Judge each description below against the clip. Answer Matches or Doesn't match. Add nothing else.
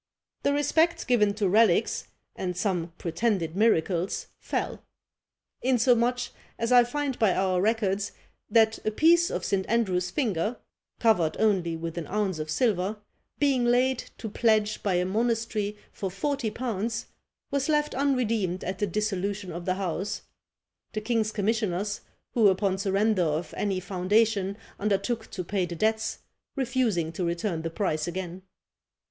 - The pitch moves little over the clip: Doesn't match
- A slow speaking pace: Doesn't match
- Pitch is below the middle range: Doesn't match